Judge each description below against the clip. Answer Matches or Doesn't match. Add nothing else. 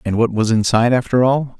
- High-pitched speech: Doesn't match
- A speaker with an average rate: Doesn't match